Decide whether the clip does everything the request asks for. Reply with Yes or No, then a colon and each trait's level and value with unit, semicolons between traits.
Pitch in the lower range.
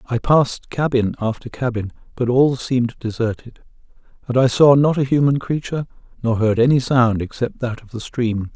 Yes: low, 125 Hz